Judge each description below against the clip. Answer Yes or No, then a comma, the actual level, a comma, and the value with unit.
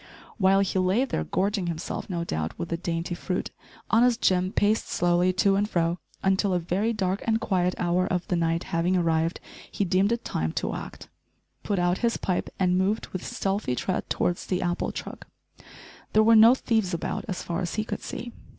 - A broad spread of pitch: No, average, 2.8 semitones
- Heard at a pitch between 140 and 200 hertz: Yes, medium, 185 Hz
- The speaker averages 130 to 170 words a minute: No, average, 195 wpm